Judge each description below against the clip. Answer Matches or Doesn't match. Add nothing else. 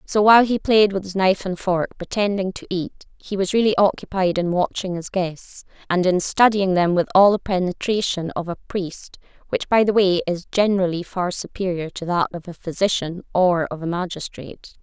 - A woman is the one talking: Matches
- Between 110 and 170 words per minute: Doesn't match